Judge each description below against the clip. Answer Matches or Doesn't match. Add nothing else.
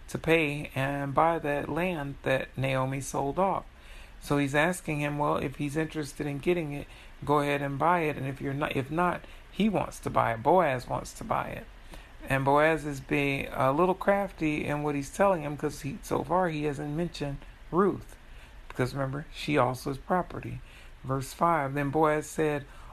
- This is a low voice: Doesn't match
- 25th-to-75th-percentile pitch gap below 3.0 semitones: Matches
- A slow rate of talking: Doesn't match